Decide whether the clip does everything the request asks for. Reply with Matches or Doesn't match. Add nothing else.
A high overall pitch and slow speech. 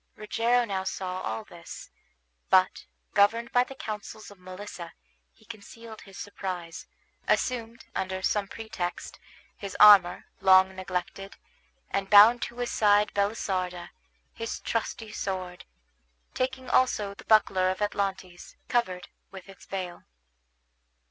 Matches